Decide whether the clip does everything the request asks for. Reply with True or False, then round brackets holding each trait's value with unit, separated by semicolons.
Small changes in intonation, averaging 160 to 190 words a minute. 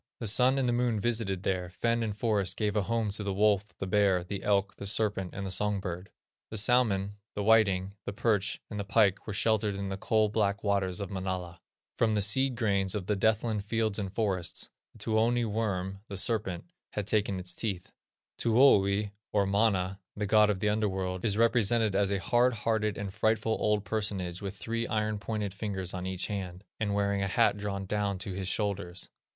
False (2.2 semitones; 200 wpm)